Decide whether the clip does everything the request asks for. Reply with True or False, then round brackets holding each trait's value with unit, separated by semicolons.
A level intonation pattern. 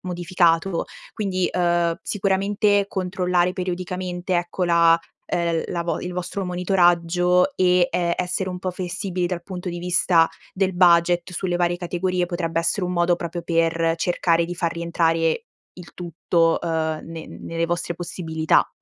True (1.3 semitones)